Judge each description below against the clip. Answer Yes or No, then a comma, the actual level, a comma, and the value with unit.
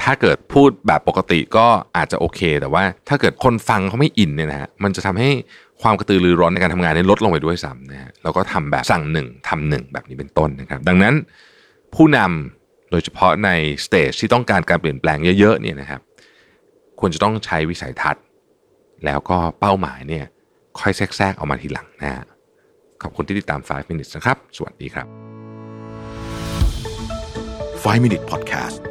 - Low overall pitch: Yes, very low, 95 Hz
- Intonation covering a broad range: Yes, wide, 5.7 semitones